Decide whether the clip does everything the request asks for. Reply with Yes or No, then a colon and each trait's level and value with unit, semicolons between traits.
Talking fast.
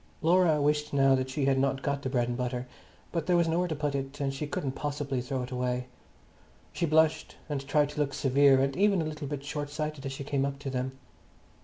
Yes: fast, 235 wpm